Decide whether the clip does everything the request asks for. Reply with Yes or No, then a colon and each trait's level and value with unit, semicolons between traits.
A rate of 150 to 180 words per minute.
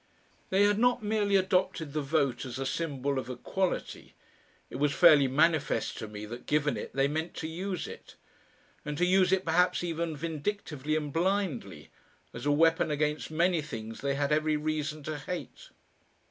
Yes: average, 175 wpm